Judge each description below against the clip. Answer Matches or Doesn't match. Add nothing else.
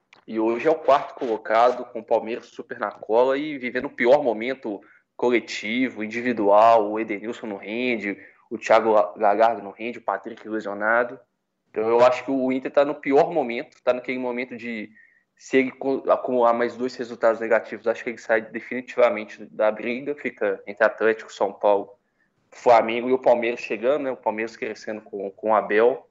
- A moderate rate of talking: Matches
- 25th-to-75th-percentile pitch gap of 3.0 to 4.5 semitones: Doesn't match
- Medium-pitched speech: Doesn't match